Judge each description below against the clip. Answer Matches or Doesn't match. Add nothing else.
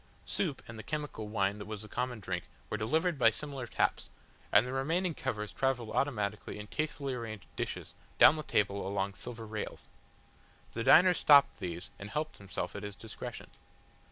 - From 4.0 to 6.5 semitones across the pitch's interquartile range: Matches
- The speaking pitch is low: Matches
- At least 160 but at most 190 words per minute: Matches